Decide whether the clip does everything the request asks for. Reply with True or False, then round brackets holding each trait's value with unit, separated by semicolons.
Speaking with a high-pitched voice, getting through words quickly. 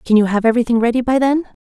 True (240 Hz; 260 wpm)